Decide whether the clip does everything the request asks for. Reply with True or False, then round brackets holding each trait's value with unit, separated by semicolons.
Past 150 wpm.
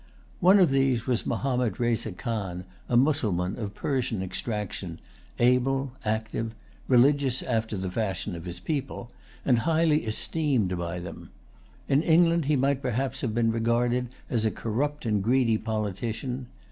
False (145 wpm)